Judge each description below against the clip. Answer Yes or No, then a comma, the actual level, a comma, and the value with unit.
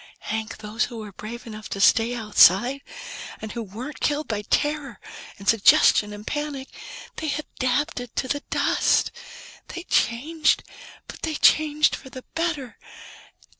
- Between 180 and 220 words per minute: No, average, 140 wpm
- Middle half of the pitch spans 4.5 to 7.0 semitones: Yes, wide, 5.4 semitones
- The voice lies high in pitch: Yes, high, 245 Hz